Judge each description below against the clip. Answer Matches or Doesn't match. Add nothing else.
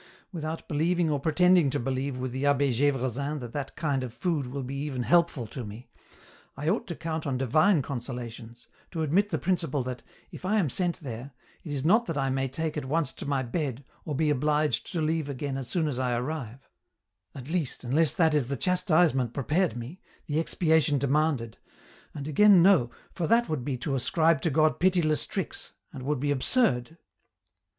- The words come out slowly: Doesn't match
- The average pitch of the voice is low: Doesn't match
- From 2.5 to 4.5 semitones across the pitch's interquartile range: Matches